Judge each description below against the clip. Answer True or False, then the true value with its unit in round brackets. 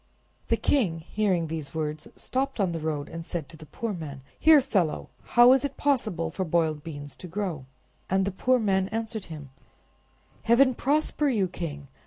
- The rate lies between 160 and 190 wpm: True (180 wpm)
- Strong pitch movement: True (6.7 semitones)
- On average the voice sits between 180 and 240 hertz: True (185 Hz)